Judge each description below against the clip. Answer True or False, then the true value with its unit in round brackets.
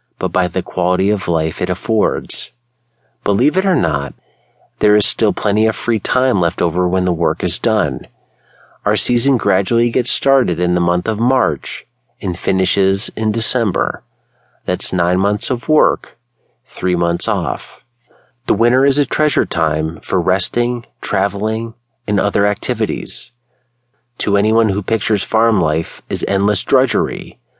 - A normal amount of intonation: True (4.5 semitones)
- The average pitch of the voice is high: False (105 Hz)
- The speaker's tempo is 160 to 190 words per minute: False (150 wpm)